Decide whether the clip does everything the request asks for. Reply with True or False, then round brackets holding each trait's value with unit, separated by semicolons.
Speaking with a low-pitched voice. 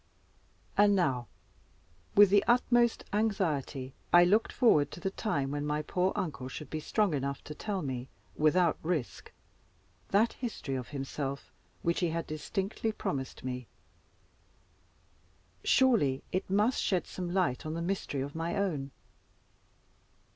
False (170 Hz)